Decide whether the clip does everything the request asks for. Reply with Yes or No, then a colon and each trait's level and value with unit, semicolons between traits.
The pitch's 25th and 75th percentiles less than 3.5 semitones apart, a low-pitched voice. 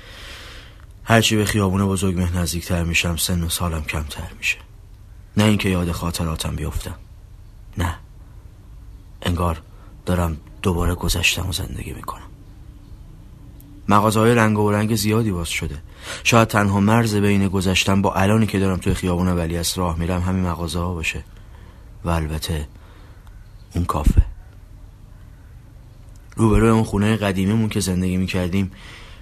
Yes: average, 3.0 semitones; very low, 95 Hz